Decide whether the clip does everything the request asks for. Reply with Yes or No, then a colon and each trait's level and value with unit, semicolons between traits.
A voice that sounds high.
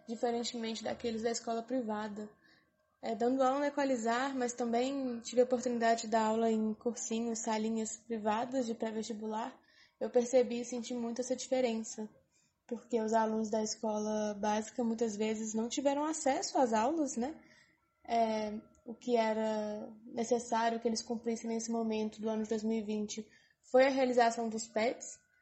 Yes: high, 230 Hz